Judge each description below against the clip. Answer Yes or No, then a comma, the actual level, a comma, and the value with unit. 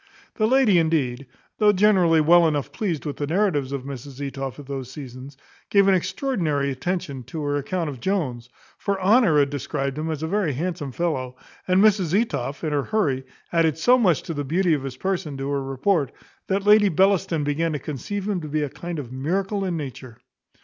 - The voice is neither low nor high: Yes, medium, 160 Hz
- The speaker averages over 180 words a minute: Yes, average, 200 wpm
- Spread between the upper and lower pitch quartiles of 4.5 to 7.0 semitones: Yes, wide, 5.5 semitones